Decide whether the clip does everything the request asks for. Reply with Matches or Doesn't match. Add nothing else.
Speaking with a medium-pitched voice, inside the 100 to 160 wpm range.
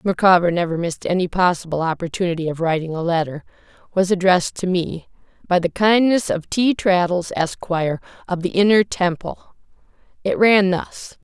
Matches